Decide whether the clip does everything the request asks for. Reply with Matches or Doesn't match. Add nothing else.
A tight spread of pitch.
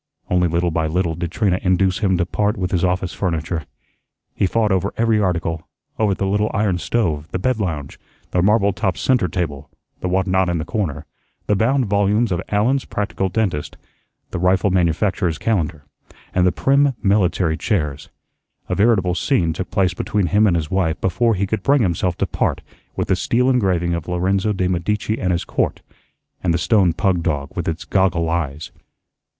Doesn't match